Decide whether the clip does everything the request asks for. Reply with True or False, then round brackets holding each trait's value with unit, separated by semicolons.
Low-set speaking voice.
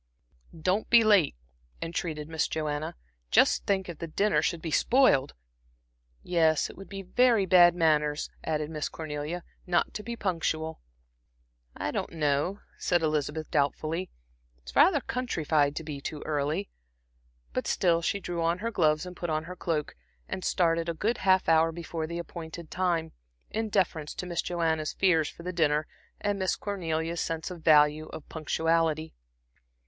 False (165 Hz)